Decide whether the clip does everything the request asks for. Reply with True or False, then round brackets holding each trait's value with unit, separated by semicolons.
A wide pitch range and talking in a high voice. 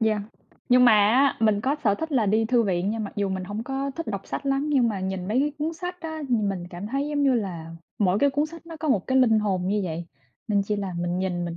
True (6.0 semitones; 220 Hz)